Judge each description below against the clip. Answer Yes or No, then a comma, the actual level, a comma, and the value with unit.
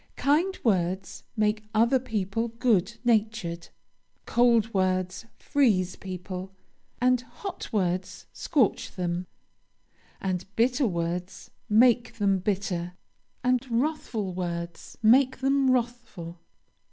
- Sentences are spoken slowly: Yes, slow, 100 wpm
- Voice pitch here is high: Yes, high, 215 Hz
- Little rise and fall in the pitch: No, average, 4.9 semitones